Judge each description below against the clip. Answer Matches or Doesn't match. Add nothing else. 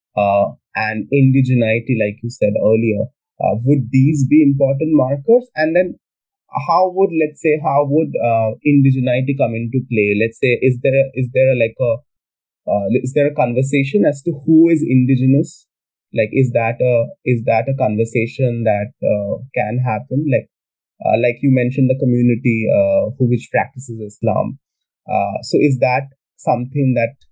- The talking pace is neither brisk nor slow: Matches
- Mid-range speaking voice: Doesn't match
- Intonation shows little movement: Doesn't match